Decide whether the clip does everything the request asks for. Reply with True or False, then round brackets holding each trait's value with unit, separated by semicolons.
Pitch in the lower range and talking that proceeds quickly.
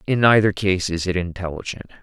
False (95 Hz; 180 wpm)